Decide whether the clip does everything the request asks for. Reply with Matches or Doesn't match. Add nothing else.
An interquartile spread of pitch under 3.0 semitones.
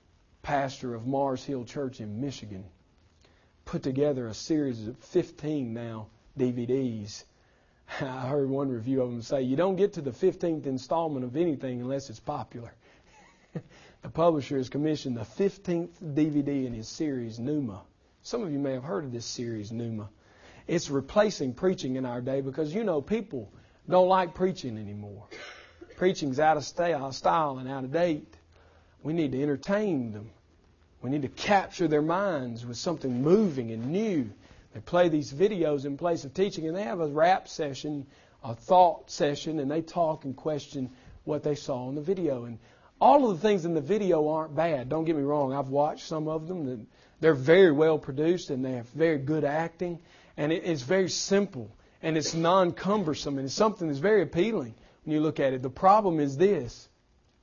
Doesn't match